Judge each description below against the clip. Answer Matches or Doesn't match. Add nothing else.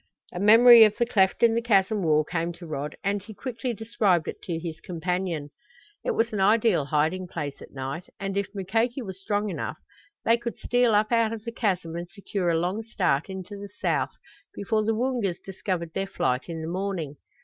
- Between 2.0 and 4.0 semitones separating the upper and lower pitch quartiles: Doesn't match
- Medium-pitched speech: Doesn't match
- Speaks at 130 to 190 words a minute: Doesn't match